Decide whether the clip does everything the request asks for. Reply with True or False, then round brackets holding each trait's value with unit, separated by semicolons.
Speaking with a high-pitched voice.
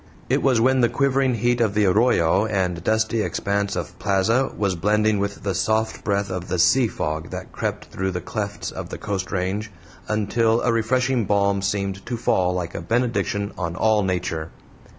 False (100 Hz)